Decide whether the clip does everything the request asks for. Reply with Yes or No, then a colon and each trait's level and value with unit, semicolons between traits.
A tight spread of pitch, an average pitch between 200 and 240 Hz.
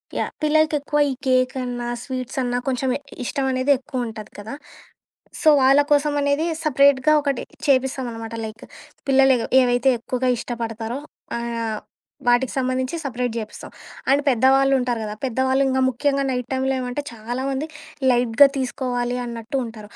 No: narrow, 2.1 semitones; very high, 255 Hz